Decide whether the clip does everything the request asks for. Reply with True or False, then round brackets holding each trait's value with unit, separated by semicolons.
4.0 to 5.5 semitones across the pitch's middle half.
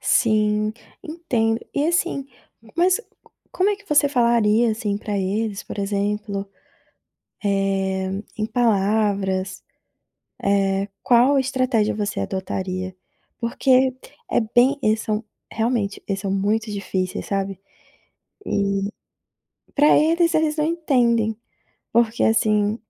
True (4.4 semitones)